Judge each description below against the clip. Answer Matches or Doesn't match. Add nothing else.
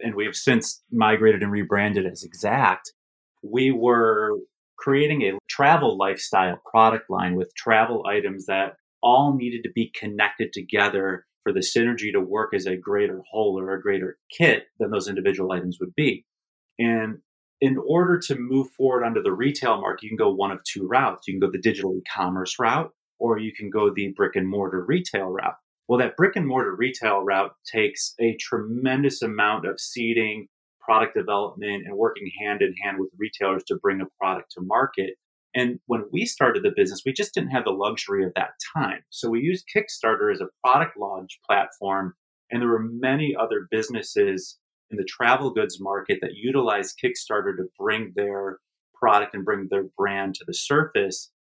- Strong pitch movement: Matches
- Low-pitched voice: Matches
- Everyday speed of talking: Matches